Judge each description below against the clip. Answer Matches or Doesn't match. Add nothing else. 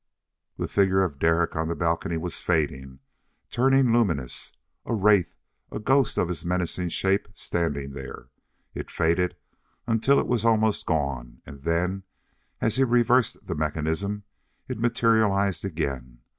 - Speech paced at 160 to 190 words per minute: Doesn't match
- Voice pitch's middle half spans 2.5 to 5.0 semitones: Doesn't match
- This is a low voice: Matches